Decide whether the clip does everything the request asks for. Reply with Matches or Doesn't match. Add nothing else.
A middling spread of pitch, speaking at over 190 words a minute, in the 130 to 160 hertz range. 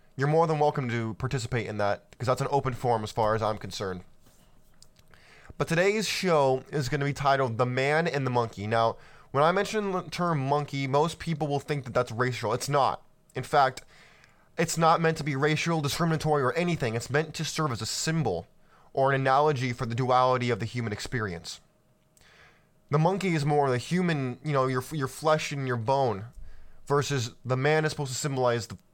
Matches